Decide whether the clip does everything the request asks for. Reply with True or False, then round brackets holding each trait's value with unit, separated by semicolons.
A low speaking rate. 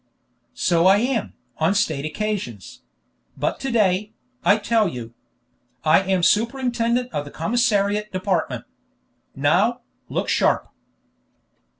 True (110 wpm)